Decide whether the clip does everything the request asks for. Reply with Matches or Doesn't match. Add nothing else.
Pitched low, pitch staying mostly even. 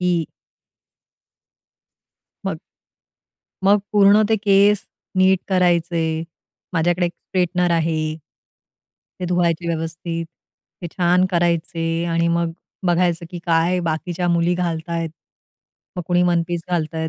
Doesn't match